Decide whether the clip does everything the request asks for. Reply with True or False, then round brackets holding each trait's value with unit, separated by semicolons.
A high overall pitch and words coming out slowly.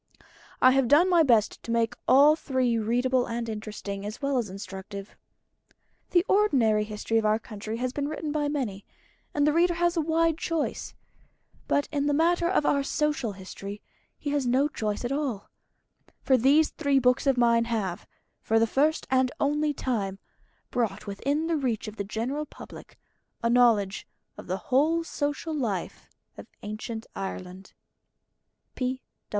False (250 Hz; 160 wpm)